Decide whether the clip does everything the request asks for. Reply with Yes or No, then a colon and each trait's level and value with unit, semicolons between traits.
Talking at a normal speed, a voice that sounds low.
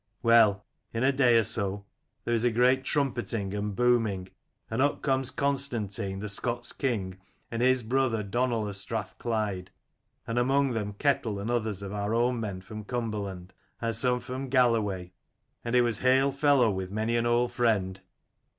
Yes: average, 170 wpm; low, 115 Hz